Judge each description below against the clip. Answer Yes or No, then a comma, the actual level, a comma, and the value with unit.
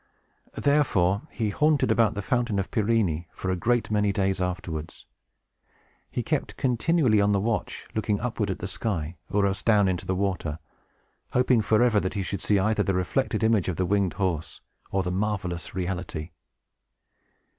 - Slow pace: No, average, 165 wpm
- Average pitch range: Yes, average, 3.4 semitones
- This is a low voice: Yes, low, 100 Hz